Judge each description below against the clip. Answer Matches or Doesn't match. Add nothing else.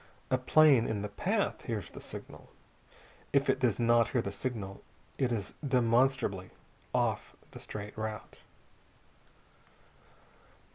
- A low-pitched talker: Matches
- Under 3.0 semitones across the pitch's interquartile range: Doesn't match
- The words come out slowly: Matches